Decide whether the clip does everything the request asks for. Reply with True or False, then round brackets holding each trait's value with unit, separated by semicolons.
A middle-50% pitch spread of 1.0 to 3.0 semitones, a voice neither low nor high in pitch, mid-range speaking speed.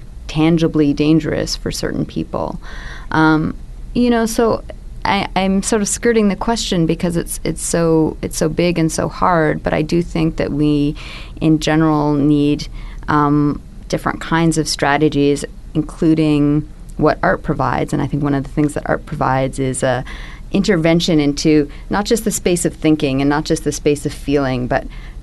True (2.4 semitones; 155 Hz; 175 wpm)